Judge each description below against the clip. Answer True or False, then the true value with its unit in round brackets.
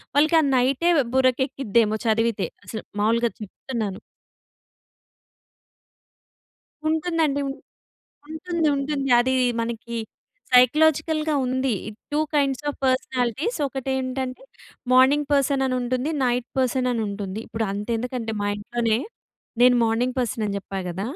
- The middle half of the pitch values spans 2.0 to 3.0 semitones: False (3.4 semitones)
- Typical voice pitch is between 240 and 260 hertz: True (255 Hz)